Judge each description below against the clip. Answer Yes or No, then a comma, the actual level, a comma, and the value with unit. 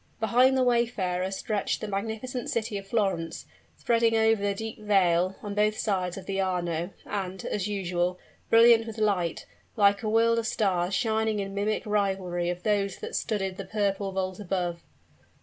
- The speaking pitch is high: Yes, high, 200 Hz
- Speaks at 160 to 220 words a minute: Yes, average, 165 wpm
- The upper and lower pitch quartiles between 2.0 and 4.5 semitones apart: Yes, average, 2.9 semitones